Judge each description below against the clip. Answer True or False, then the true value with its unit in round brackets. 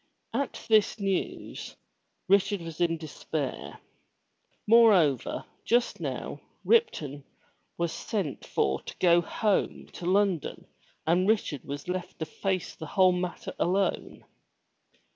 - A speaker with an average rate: False (115 wpm)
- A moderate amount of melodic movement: True (4.0 semitones)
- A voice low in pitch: False (180 Hz)